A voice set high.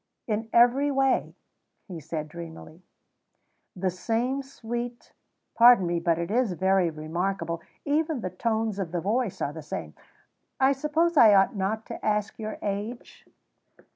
Yes: high, 210 Hz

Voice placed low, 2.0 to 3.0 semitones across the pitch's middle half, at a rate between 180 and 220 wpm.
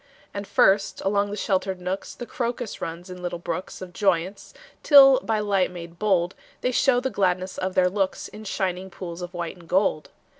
No: high, 190 Hz; narrow, 2.5 semitones; average, 190 wpm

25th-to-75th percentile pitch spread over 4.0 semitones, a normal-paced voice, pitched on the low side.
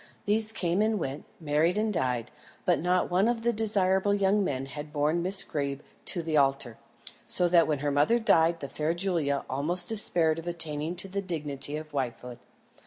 No: average, 4.8 semitones; average, 185 wpm; medium, 165 Hz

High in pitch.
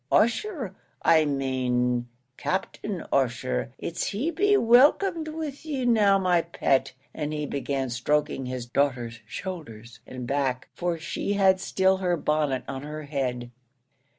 No: medium, 150 Hz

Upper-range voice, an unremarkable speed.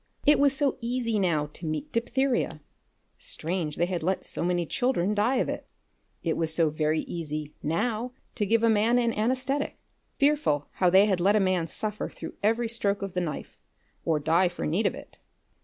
Yes: high, 195 Hz; average, 190 wpm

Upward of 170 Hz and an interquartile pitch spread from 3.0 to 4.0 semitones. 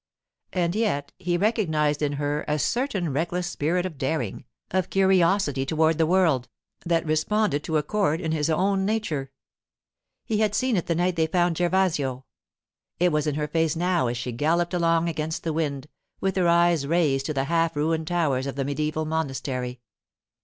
No: medium, 160 Hz; average, 3.3 semitones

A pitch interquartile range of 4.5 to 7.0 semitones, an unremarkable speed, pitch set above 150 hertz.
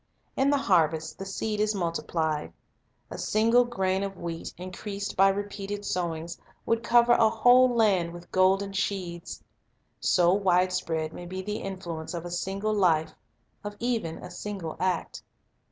No: average, 3.3 semitones; average, 155 wpm; high, 190 Hz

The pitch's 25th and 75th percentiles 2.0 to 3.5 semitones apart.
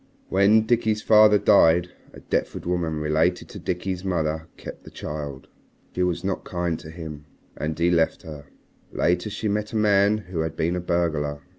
No: average, 3.9 semitones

